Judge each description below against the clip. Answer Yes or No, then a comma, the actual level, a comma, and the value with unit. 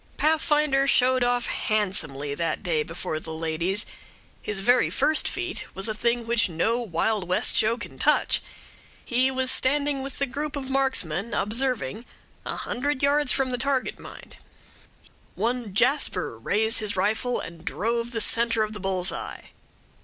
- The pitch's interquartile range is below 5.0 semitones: No, average, 5.3 semitones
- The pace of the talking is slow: No, average, 155 wpm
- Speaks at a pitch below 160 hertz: No, high, 235 Hz